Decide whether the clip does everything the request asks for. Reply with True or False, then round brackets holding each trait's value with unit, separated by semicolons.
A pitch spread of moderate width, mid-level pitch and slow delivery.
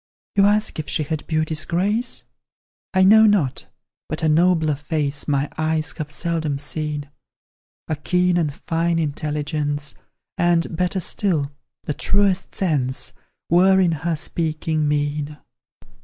True (3.1 semitones; 160 Hz; 130 wpm)